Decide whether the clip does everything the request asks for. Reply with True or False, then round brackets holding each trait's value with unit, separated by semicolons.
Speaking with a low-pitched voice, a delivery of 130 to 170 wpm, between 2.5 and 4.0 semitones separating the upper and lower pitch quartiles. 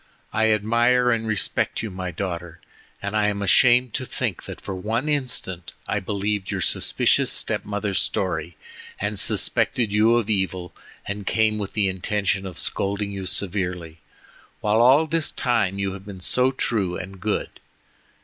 True (105 Hz; 160 wpm; 3.1 semitones)